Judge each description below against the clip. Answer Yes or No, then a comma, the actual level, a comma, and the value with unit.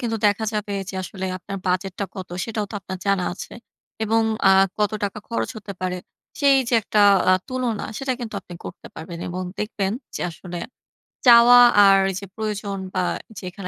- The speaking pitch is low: No, high, 200 Hz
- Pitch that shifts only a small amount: No, average, 3.0 semitones